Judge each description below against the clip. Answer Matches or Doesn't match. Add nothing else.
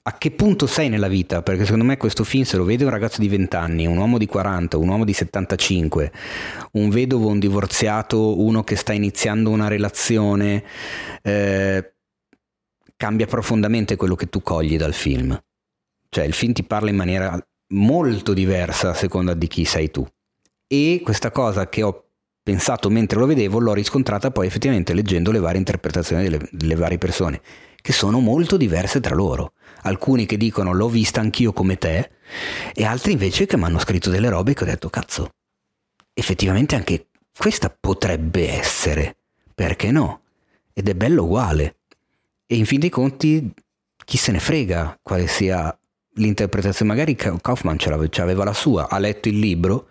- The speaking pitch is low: Matches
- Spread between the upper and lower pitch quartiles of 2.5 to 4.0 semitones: Matches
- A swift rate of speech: Matches